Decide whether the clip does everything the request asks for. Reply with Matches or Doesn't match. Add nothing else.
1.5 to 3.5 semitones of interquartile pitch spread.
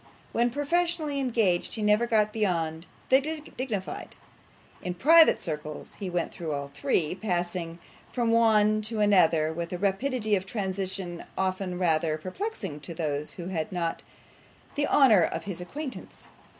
Doesn't match